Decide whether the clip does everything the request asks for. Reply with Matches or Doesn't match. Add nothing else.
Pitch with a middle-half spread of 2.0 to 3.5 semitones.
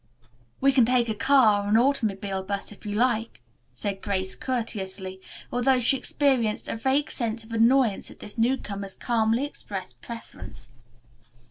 Doesn't match